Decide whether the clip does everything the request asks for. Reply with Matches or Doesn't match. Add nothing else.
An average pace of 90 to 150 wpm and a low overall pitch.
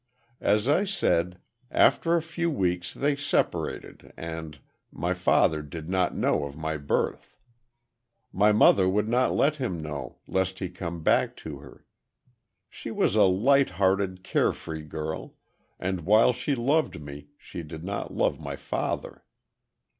Matches